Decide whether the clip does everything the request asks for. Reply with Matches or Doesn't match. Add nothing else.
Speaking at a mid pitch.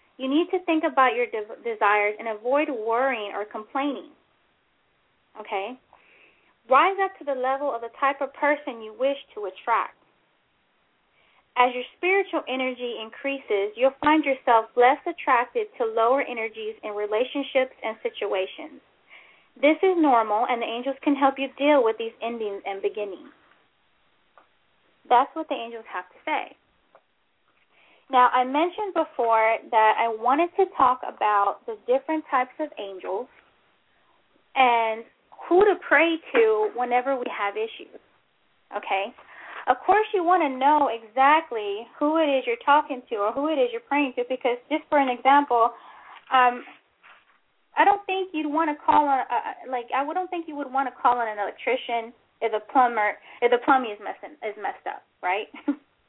Doesn't match